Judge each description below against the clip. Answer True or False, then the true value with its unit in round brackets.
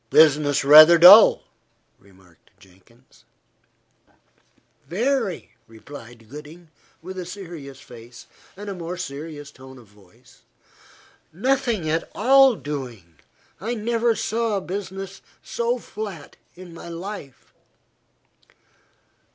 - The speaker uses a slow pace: True (95 wpm)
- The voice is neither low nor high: True (165 Hz)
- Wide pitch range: True (7.4 semitones)